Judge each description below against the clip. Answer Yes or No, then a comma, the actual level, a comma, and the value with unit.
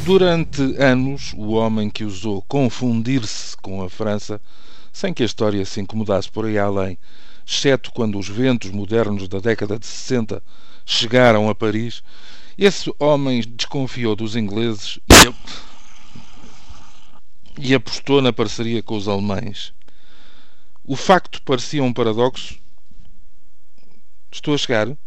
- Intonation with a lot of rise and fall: No, average, 3.9 semitones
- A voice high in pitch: No, low, 115 Hz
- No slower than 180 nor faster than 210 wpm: No, slow, 120 wpm